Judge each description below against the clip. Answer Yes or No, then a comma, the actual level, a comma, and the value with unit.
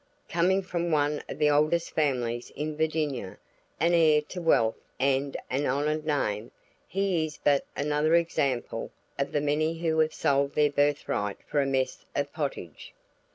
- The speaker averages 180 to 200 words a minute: No, average, 160 wpm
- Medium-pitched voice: Yes, medium, 150 Hz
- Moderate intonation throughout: No, narrow, 2.3 semitones